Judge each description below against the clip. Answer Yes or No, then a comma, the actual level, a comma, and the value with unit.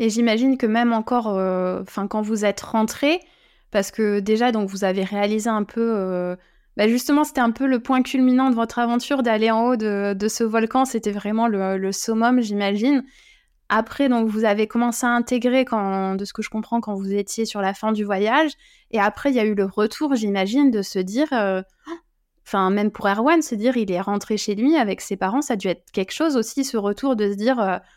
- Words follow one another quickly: Yes, fast, 225 wpm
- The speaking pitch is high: Yes, high, 220 Hz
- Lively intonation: No, average, 3.5 semitones